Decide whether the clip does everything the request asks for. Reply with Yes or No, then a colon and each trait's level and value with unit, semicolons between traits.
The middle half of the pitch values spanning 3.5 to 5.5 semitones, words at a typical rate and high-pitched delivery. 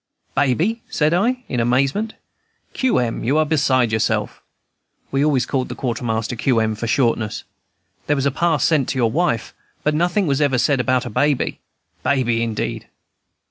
No: average, 4.3 semitones; average, 170 wpm; low, 135 Hz